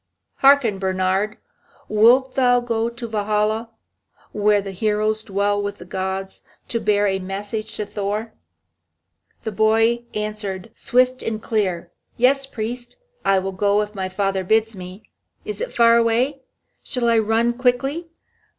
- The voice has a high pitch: Yes, high, 215 Hz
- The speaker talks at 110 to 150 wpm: Yes, average, 140 wpm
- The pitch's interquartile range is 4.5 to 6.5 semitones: No, average, 2.9 semitones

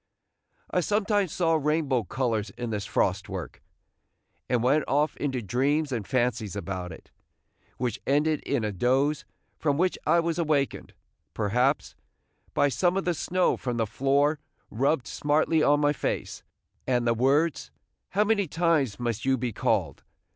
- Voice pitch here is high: No, medium, 140 Hz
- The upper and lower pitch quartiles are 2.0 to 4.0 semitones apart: No, average, 4.7 semitones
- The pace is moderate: Yes, average, 155 wpm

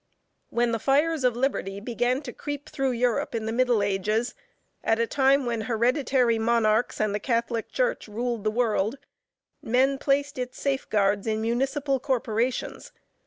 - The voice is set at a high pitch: Yes, high, 240 Hz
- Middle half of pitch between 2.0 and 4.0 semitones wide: Yes, average, 3.2 semitones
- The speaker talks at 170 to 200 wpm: No, average, 155 wpm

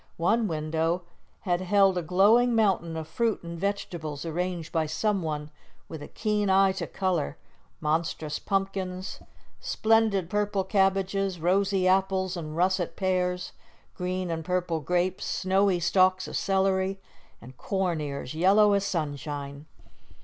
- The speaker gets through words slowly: Yes, slow, 130 wpm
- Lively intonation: No, average, 3.1 semitones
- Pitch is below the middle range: No, medium, 185 Hz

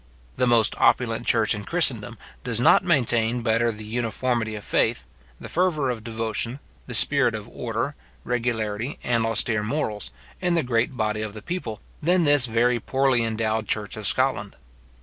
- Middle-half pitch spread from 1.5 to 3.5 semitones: Yes, average, 2.7 semitones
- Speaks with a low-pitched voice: Yes, low, 115 Hz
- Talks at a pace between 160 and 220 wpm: Yes, average, 165 wpm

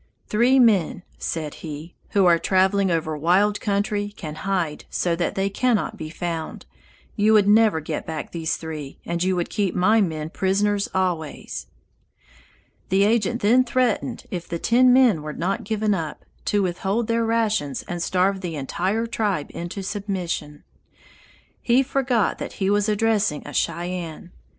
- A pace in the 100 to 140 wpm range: No, average, 155 wpm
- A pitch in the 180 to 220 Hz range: Yes, high, 190 Hz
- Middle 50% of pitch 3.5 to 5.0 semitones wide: Yes, average, 4.1 semitones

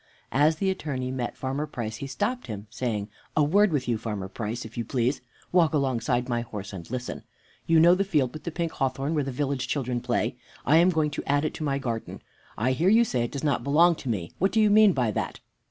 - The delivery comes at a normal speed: No, fast, 240 wpm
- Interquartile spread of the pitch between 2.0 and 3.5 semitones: No, average, 5.1 semitones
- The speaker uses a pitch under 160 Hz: Yes, low, 135 Hz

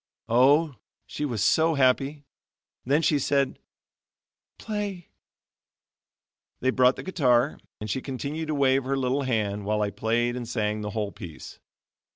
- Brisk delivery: No, average, 145 wpm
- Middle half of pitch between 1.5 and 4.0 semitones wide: No, average, 4.4 semitones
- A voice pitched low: Yes, low, 130 Hz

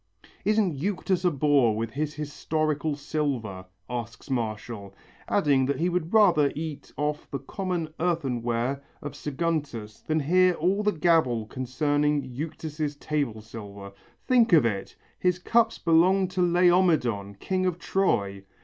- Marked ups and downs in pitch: Yes, wide, 6.2 semitones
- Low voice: No, medium, 150 Hz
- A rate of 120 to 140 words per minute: Yes, slow, 135 wpm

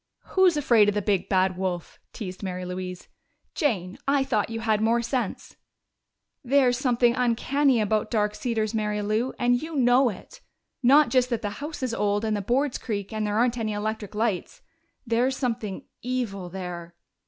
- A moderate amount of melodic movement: Yes, average, 3.5 semitones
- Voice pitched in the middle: No, high, 225 Hz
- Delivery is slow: No, average, 175 wpm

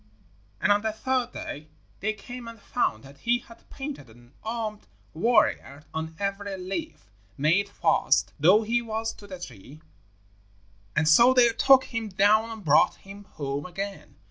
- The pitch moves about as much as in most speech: No, wide, 6.1 semitones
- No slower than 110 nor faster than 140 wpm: No, average, 160 wpm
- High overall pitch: Yes, high, 205 Hz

